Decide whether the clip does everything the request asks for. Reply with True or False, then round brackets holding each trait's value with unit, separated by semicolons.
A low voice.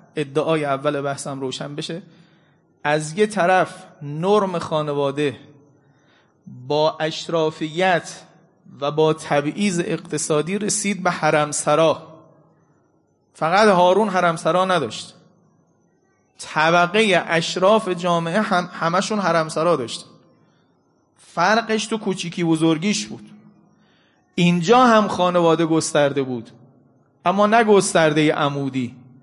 False (170 Hz)